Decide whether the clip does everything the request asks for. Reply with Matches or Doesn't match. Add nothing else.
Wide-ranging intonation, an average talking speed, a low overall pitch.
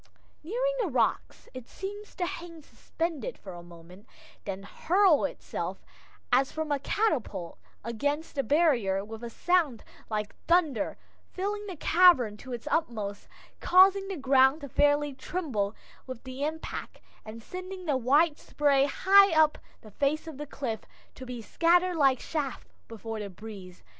Doesn't match